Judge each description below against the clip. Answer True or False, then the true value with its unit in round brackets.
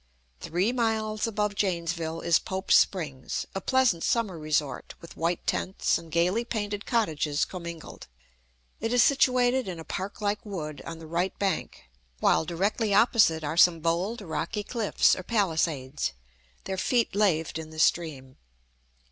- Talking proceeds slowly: False (150 wpm)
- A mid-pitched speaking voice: True (180 Hz)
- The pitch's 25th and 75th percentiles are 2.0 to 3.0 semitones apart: False (4.7 semitones)